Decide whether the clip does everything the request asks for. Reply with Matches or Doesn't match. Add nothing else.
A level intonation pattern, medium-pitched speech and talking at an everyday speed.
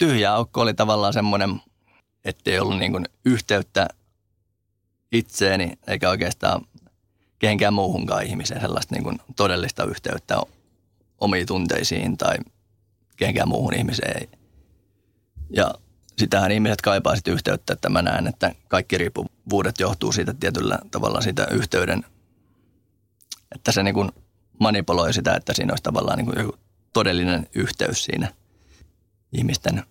Doesn't match